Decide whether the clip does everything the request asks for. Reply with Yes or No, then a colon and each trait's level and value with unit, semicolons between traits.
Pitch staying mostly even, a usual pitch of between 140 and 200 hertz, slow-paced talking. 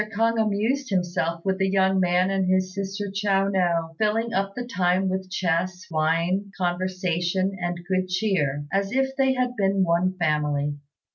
No: narrow, 2.2 semitones; medium, 185 Hz; average, 160 wpm